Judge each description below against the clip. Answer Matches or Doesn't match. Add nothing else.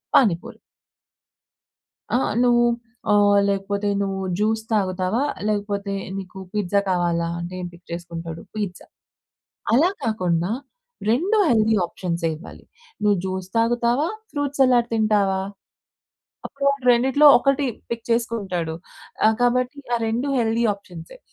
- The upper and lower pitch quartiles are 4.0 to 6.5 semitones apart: Matches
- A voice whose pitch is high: Matches